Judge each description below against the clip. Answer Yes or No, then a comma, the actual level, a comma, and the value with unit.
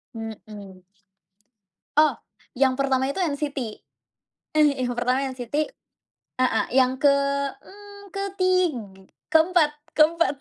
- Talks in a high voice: Yes, very high, 285 Hz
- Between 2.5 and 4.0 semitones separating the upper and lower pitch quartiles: No, average, 4.8 semitones